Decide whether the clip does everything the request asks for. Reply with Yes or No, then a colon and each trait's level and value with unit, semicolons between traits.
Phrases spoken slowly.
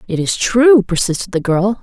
No: average, 195 wpm